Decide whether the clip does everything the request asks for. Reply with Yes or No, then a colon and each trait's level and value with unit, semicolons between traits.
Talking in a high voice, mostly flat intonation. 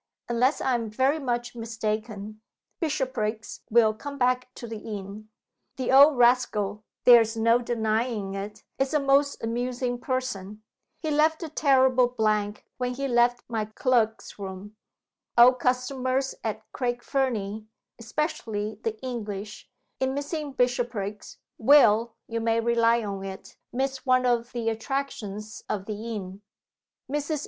No: high, 235 Hz; average, 3.2 semitones